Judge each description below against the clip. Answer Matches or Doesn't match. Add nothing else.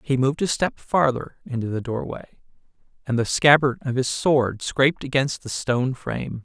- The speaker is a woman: Doesn't match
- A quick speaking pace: Doesn't match